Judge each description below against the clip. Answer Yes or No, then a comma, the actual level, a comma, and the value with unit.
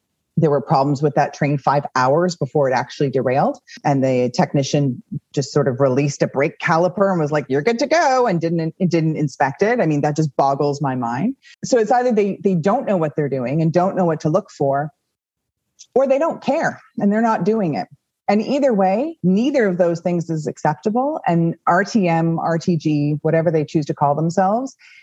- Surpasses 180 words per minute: Yes, fast, 205 wpm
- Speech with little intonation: No, average, 5.2 semitones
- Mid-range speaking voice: Yes, medium, 165 Hz